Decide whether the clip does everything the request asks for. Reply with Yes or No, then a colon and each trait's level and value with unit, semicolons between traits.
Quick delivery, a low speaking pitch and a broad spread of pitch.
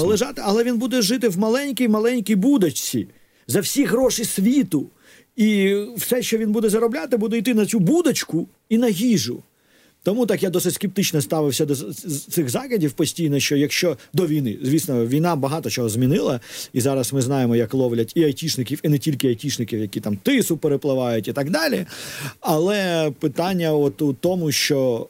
No: fast, 165 wpm; medium, 170 Hz; wide, 8.0 semitones